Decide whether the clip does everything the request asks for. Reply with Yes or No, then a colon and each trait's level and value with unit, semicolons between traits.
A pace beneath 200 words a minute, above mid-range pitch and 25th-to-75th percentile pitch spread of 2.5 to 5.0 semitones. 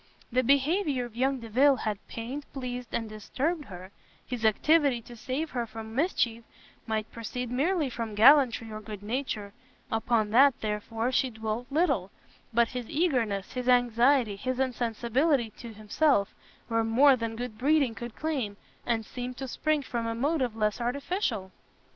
Yes: average, 155 wpm; high, 245 Hz; average, 3.4 semitones